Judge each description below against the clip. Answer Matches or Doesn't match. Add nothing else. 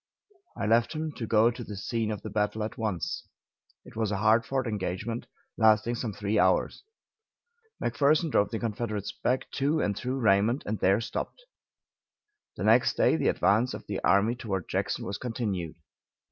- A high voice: Doesn't match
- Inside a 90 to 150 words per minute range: Doesn't match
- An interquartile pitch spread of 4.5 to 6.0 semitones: Doesn't match